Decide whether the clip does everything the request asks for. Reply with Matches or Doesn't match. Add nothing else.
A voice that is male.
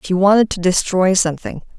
Doesn't match